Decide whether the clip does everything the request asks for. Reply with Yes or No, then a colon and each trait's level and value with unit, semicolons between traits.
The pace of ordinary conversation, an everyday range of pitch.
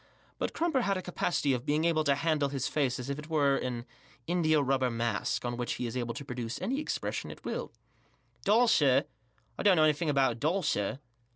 No: fast, 210 wpm; average, 4.8 semitones